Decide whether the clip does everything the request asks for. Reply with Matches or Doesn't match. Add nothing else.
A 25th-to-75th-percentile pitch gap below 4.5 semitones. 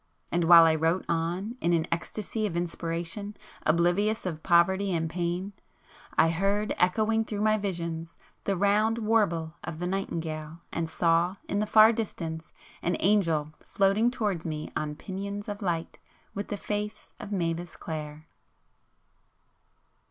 Matches